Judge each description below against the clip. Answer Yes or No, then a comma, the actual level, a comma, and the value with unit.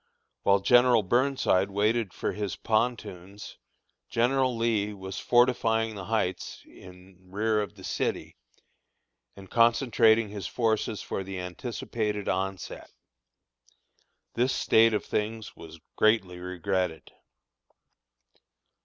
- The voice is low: Yes, low, 105 Hz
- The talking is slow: Yes, slow, 105 wpm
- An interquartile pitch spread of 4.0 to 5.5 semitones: No, average, 3.3 semitones